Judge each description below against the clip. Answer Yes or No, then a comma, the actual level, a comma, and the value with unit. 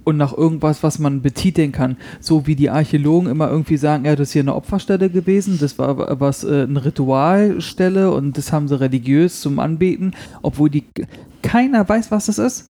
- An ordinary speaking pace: No, fast, 195 wpm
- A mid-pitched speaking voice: Yes, medium, 155 Hz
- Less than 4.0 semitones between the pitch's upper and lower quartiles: No, average, 4.5 semitones